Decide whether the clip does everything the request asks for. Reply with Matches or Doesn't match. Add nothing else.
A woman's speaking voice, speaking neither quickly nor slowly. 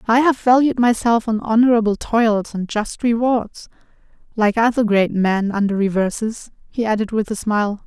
Matches